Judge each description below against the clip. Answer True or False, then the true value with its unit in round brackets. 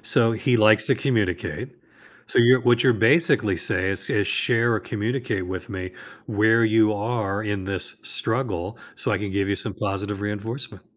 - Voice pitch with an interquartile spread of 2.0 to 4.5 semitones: True (2.9 semitones)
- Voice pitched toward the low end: True (105 Hz)